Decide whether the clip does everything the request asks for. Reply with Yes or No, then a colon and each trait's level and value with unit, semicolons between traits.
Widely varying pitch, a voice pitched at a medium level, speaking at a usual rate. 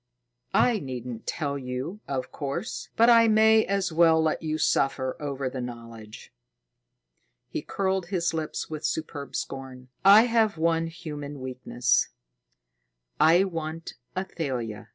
No: wide, 6.0 semitones; medium, 155 Hz; slow, 130 wpm